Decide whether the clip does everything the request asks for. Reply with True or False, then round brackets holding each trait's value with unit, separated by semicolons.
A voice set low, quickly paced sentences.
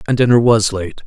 True (110 Hz; 225 wpm)